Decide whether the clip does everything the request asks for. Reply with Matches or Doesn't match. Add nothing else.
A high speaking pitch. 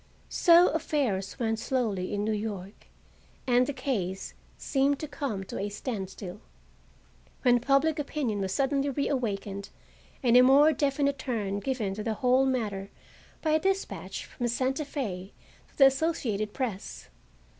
Matches